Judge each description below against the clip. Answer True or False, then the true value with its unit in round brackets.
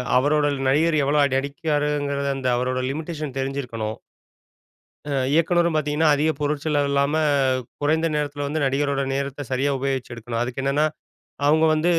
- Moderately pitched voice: True (145 Hz)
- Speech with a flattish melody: True (2.0 semitones)